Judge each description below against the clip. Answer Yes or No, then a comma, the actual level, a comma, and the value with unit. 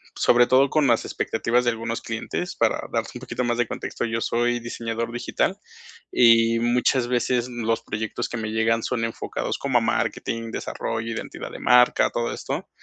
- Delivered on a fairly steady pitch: Yes, narrow, 1.1 semitones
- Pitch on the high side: No, low, 115 Hz